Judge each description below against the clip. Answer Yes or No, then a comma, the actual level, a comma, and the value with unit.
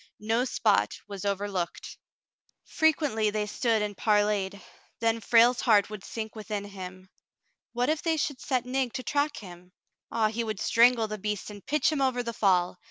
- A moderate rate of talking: Yes, average, 175 wpm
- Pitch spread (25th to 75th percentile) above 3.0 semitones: Yes, average, 3.6 semitones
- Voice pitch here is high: Yes, high, 220 Hz